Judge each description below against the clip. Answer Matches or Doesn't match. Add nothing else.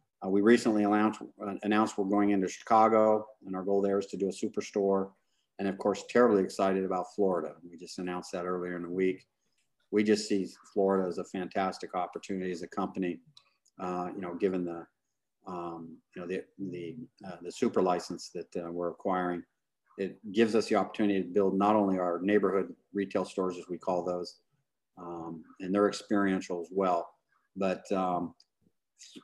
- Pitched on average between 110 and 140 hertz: Doesn't match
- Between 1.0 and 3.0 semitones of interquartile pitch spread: Matches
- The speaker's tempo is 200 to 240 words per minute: Doesn't match